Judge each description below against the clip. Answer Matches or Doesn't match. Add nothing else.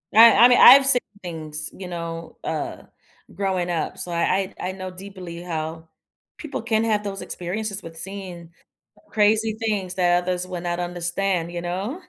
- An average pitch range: Matches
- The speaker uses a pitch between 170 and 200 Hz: Matches